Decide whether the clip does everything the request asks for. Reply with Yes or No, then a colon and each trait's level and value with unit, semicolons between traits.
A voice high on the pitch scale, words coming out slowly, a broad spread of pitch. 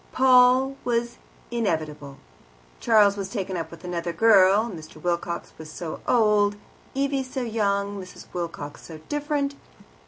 Yes: high, 200 Hz; slow, 130 wpm; wide, 6.0 semitones